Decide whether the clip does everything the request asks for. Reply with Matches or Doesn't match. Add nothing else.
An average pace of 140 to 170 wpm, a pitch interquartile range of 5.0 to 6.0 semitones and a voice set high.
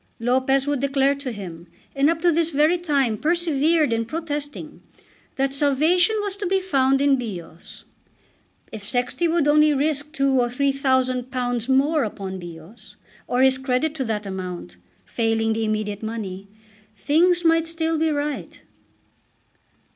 Matches